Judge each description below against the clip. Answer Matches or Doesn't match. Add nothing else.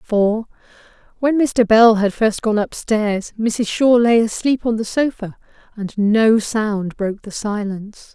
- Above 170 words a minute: Doesn't match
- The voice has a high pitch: Matches